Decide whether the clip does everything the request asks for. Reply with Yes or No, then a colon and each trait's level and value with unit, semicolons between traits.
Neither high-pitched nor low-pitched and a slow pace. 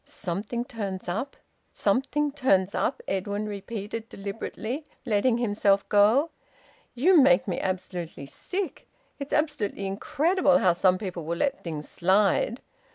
No: high, 210 Hz; slow, 125 wpm